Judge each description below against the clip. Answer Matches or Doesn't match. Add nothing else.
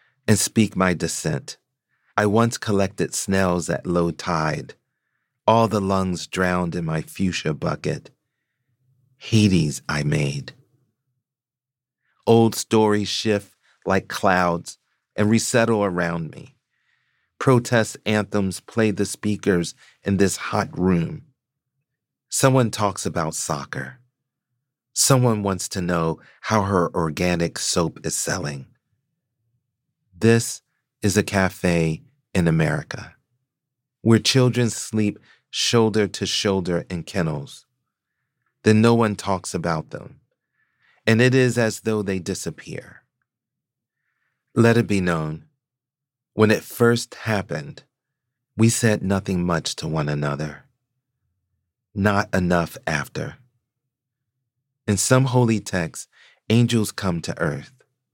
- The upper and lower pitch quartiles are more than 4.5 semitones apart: Matches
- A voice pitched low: Matches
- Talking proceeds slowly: Matches